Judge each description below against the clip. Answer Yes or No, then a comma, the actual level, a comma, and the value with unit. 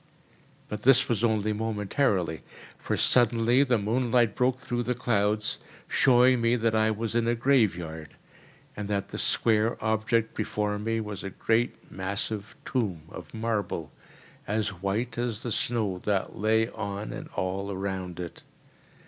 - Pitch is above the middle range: No, low, 110 Hz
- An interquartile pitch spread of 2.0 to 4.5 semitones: Yes, average, 2.8 semitones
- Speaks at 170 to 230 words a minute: No, average, 150 wpm